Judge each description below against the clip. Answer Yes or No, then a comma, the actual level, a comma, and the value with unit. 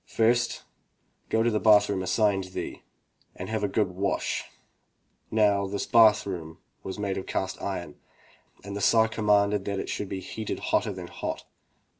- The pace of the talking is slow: No, average, 180 wpm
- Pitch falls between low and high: No, low, 100 Hz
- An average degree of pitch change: No, narrow, 2.2 semitones